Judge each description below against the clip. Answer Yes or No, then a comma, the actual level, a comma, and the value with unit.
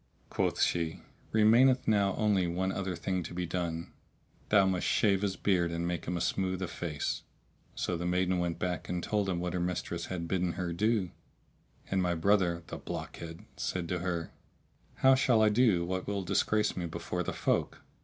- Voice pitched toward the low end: Yes, very low, 90 Hz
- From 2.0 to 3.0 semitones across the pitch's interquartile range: Yes, narrow, 2.5 semitones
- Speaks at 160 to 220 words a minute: Yes, average, 190 wpm